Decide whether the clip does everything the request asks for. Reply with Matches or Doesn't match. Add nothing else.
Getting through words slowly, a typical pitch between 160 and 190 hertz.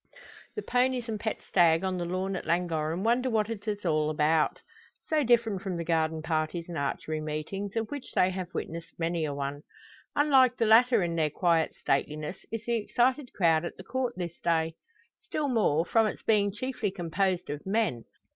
Doesn't match